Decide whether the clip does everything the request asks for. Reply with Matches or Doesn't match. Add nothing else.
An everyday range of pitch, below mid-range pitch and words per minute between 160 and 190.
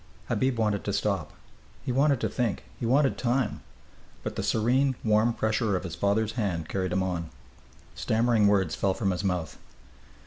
Matches